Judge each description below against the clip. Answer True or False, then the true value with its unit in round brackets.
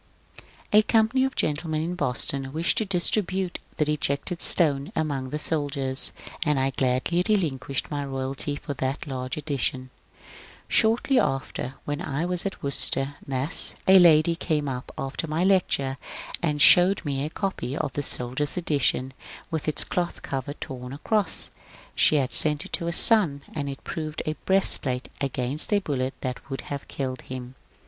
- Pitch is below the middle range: False (145 Hz)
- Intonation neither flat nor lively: True (4.3 semitones)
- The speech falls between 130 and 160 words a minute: False (170 wpm)